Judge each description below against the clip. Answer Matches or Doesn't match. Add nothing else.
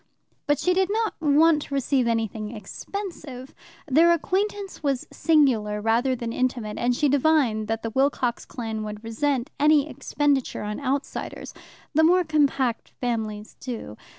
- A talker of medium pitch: Doesn't match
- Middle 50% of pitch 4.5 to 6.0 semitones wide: Matches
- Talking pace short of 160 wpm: Matches